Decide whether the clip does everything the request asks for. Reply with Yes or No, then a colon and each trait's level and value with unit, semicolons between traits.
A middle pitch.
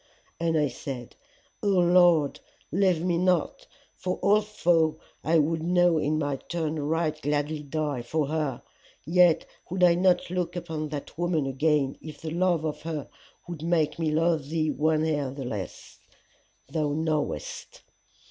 Yes: medium, 160 Hz